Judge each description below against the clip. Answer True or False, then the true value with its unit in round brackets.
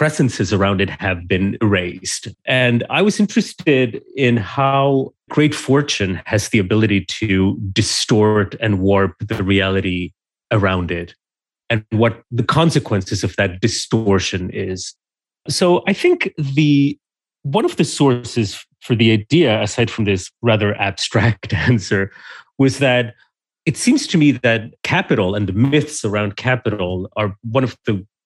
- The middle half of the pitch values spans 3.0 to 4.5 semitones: False (5.4 semitones)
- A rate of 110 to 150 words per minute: True (140 wpm)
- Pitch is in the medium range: False (115 Hz)